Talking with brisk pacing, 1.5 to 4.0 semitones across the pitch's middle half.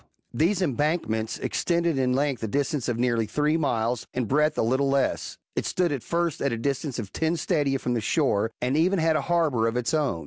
No: fast, 215 wpm; average, 4.8 semitones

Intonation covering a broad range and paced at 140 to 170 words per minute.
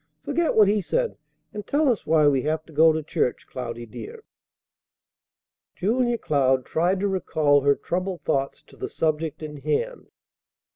Yes: wide, 6.4 semitones; average, 160 wpm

